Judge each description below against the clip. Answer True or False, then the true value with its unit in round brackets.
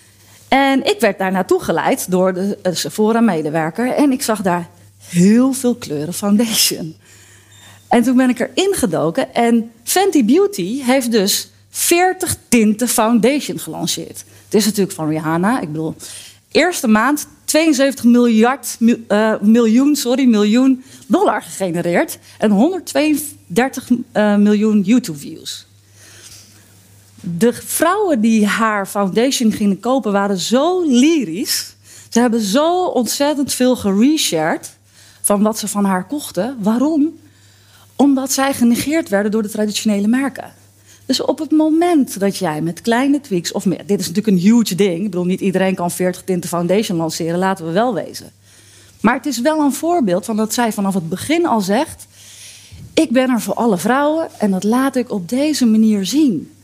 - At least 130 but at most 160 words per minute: True (155 wpm)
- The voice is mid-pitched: False (215 Hz)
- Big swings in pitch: True (6.1 semitones)